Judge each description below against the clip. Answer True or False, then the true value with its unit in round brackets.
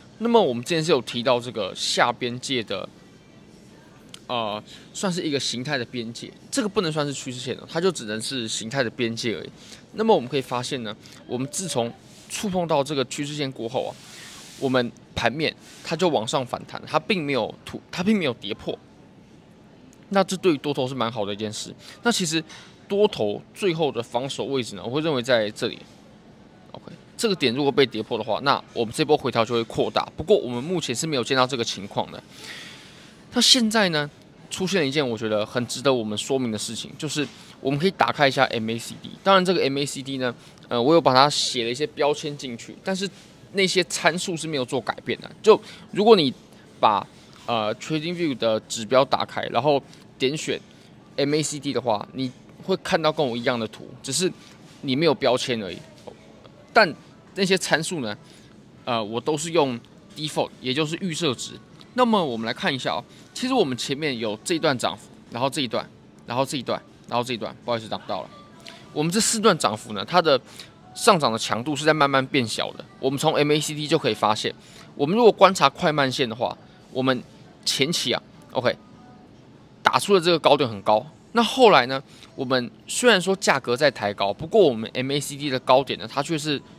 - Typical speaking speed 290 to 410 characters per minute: True (310 characters per minute)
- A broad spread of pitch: True (6.3 semitones)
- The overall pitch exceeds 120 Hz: True (140 Hz)